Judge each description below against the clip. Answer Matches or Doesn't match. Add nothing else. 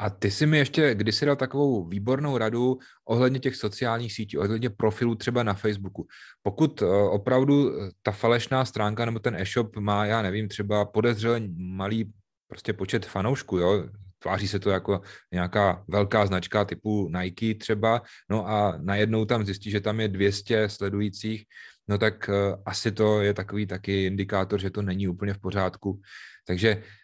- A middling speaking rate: Matches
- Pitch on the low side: Matches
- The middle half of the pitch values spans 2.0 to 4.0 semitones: Matches